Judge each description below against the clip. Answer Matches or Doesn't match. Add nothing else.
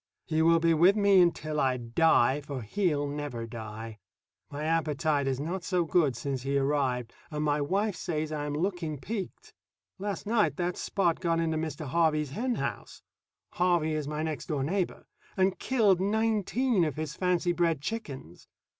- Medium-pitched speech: Matches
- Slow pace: Doesn't match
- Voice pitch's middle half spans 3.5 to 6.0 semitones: Matches